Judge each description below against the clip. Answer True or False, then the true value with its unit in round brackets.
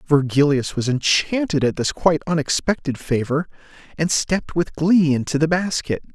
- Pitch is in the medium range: True (155 Hz)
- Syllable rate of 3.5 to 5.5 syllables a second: True (5.1 syllables/s)